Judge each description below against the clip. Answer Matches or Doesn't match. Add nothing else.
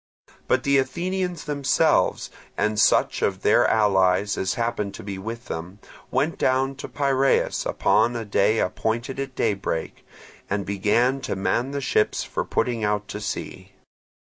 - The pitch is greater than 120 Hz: Doesn't match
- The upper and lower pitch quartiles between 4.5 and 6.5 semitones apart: Matches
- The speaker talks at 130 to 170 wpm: Matches